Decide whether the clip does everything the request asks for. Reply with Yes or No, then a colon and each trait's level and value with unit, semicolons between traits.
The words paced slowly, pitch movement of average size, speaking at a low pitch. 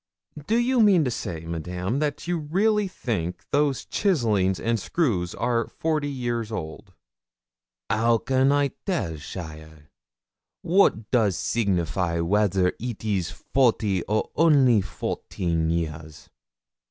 No: slow, 120 wpm; wide, 8.3 semitones; low, 110 Hz